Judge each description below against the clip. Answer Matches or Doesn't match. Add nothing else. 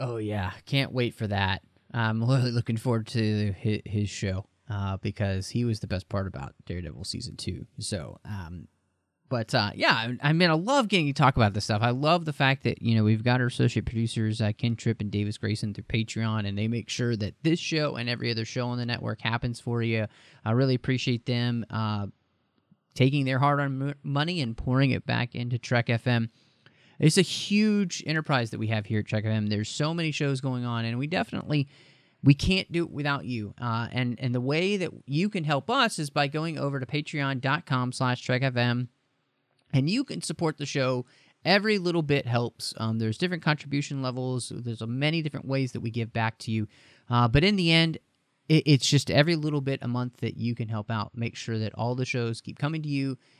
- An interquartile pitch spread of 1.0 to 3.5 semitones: Doesn't match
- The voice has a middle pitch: Doesn't match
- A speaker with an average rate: Doesn't match